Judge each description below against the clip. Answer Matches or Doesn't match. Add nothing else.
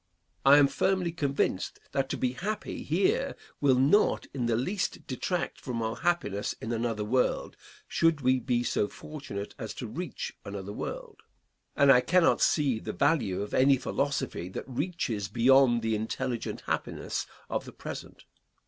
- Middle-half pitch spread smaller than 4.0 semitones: Doesn't match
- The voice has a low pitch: Matches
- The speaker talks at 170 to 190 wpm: Doesn't match